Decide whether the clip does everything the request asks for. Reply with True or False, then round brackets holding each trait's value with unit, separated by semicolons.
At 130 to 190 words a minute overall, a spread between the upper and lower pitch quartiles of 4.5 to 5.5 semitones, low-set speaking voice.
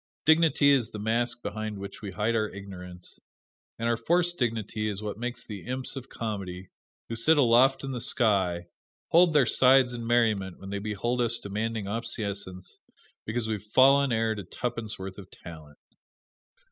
False (170 wpm; 3.5 semitones; 110 Hz)